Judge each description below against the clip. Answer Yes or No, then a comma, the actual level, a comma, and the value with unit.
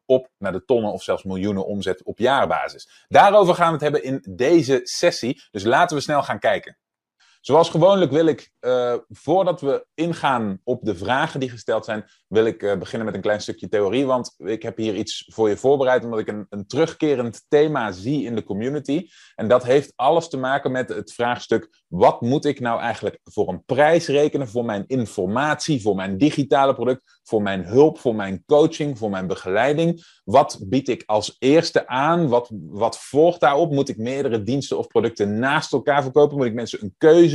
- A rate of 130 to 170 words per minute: No, fast, 200 wpm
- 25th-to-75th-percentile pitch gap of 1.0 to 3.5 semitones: No, average, 5.3 semitones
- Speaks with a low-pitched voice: Yes, low, 130 Hz